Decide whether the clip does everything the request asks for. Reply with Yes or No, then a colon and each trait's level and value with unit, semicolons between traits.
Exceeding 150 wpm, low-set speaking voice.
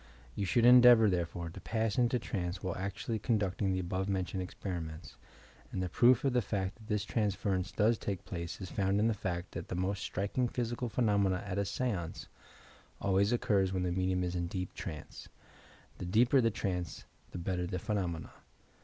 Yes: average, 185 wpm; very low, 95 Hz